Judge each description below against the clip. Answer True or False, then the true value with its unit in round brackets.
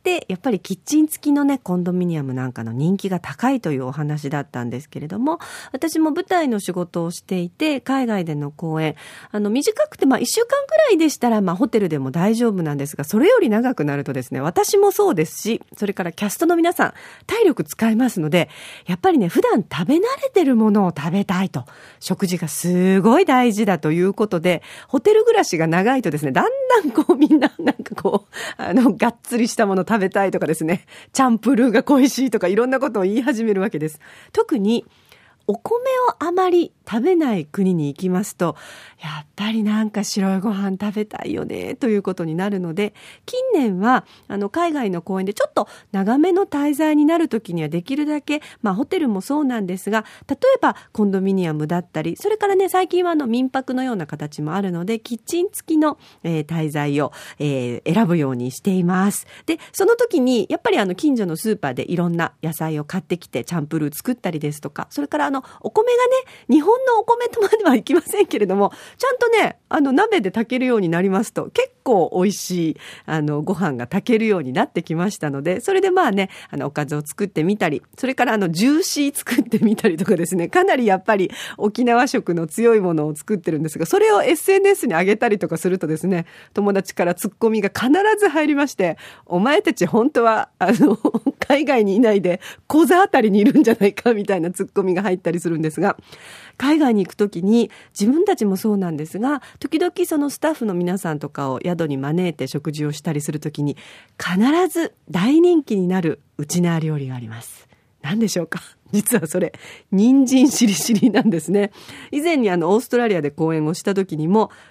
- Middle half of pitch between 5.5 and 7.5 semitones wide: False (8.4 semitones)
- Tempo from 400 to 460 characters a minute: True (405 characters per minute)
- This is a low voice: False (210 Hz)